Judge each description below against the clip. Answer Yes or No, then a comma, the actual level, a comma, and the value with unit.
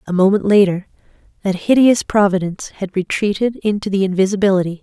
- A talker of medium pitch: No, high, 195 Hz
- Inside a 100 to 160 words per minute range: Yes, slow, 135 wpm